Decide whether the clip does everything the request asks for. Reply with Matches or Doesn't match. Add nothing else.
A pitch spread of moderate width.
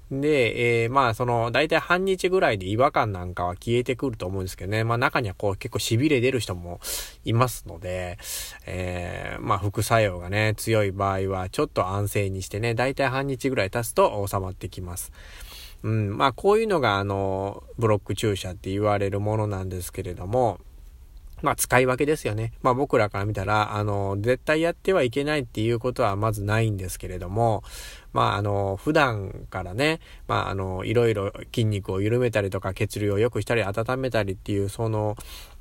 Matches